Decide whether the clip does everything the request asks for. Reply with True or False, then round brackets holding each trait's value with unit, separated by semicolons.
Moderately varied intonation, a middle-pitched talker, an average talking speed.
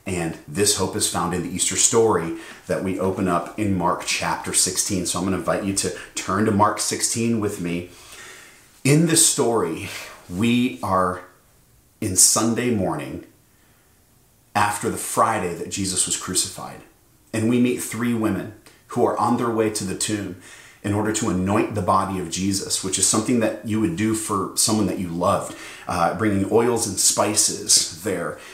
False (3.3 semitones; 100 Hz; 175 wpm)